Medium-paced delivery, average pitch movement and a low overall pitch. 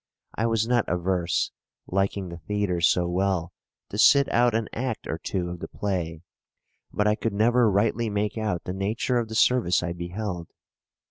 Yes: average, 180 wpm; average, 4.2 semitones; low, 100 Hz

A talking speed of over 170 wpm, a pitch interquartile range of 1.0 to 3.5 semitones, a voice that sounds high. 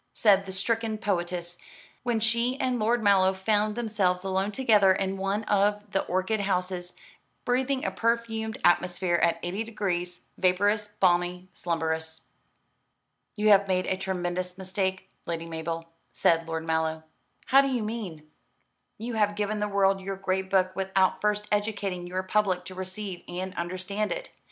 No: average, 150 wpm; average, 2.8 semitones; high, 195 Hz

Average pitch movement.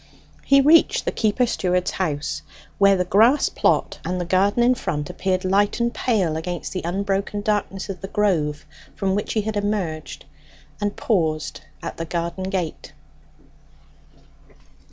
Yes: average, 3.2 semitones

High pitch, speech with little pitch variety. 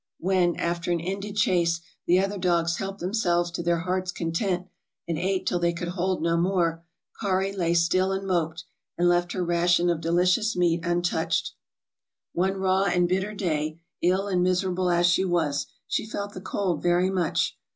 No: medium, 175 Hz; narrow, 1.8 semitones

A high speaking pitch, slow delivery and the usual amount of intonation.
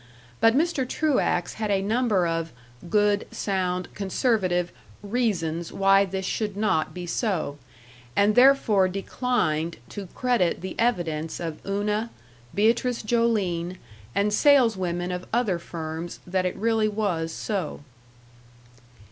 Yes: high, 195 Hz; slow, 120 wpm; average, 4.2 semitones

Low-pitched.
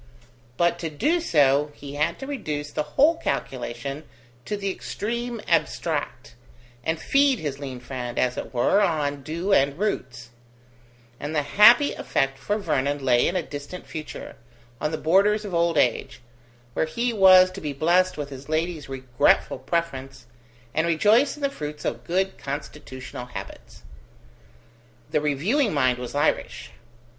No: medium, 155 Hz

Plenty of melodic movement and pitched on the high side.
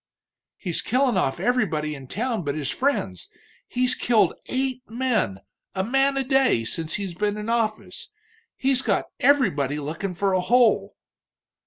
Yes: wide, 8.1 semitones; high, 215 Hz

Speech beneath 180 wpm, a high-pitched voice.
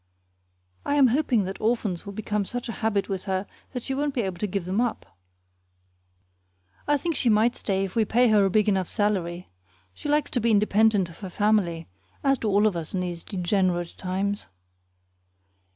No: average, 195 wpm; high, 205 Hz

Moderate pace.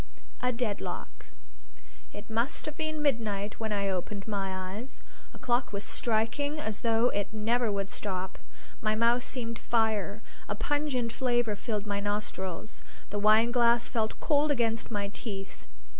Yes: average, 145 wpm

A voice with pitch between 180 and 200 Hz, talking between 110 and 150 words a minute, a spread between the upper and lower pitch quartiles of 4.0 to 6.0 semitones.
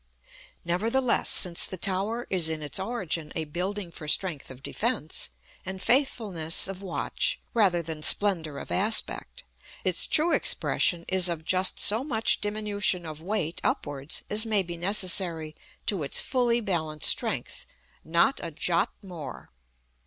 Yes: medium, 185 Hz; average, 145 wpm; average, 4.6 semitones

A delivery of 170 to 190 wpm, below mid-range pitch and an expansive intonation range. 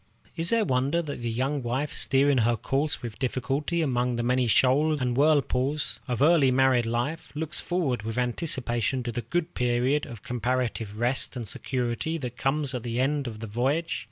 No: average, 180 wpm; low, 130 Hz; average, 3.4 semitones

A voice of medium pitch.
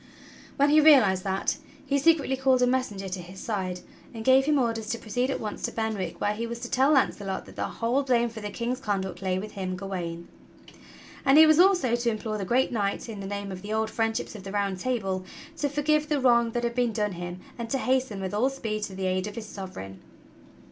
No: high, 220 Hz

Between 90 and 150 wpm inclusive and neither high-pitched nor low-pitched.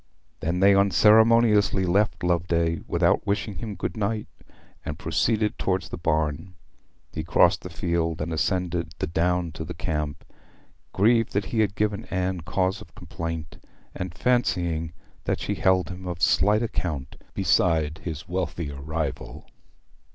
No: average, 145 wpm; very low, 90 Hz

